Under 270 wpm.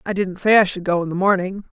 No: fast, 300 wpm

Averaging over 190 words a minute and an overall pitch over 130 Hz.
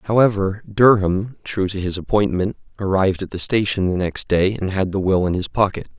No: average, 200 wpm; low, 100 Hz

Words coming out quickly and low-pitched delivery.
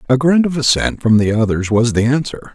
Yes: fast, 235 wpm; low, 130 Hz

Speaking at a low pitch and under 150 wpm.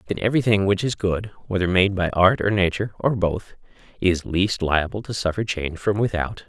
No: very low, 95 Hz; average, 195 wpm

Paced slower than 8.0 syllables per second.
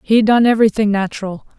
Yes: 6.5 syllables/s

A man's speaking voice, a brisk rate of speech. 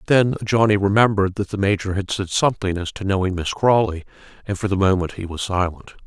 Yes: male; fast, 210 wpm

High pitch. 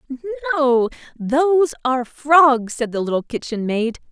Yes: very high, 275 Hz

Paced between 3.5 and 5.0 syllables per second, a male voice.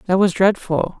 Yes: 4.9 syllables/s; male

